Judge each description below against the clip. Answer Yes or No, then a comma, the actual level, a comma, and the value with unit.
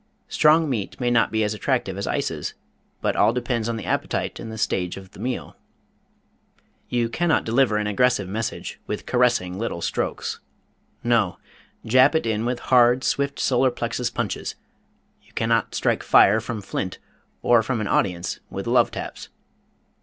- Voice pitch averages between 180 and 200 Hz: No, low, 115 Hz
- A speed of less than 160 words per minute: No, average, 165 wpm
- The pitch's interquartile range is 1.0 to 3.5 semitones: Yes, average, 2.9 semitones